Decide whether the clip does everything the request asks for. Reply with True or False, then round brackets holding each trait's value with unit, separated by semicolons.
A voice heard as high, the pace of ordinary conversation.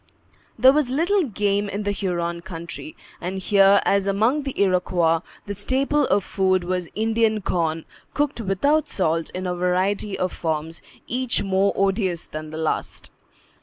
True (195 Hz; 155 wpm)